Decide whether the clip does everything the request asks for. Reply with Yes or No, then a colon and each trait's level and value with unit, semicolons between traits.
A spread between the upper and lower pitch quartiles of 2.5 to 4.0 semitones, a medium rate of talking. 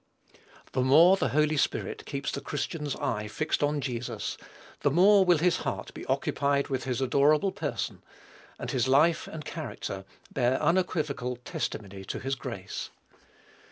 Yes: average, 3.5 semitones; average, 150 wpm